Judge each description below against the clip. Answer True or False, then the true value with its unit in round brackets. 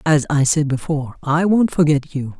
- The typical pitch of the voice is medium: True (150 Hz)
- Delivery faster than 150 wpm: True (200 wpm)